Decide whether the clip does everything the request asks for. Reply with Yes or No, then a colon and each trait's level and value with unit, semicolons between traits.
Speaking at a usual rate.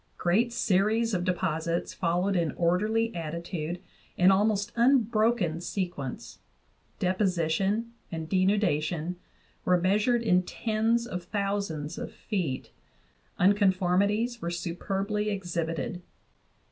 No: slow, 105 wpm